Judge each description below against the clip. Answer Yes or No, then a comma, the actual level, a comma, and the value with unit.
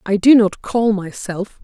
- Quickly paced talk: No, average, 185 wpm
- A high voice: Yes, high, 205 Hz